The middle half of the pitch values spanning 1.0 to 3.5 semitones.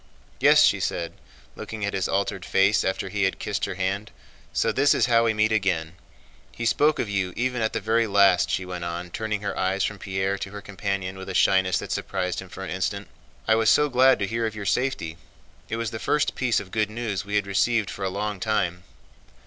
Yes: average, 2.7 semitones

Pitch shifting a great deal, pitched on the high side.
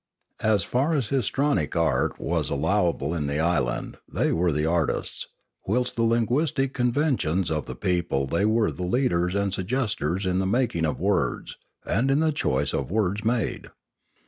No: wide, 6.8 semitones; low, 100 Hz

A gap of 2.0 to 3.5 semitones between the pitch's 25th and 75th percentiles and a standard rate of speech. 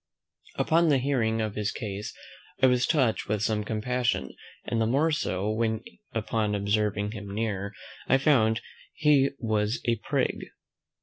Yes: average, 3.2 semitones; average, 145 wpm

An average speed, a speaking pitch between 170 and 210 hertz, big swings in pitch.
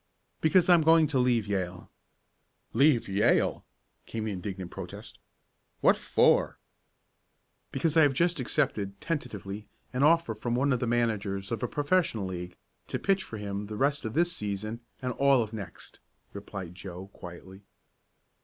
No: average, 155 wpm; low, 110 Hz; wide, 6.3 semitones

